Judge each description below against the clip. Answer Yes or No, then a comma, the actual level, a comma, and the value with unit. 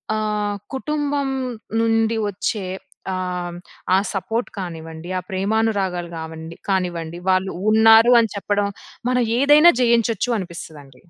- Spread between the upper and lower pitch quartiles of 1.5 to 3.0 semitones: No, average, 4.3 semitones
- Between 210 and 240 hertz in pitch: No, high, 200 Hz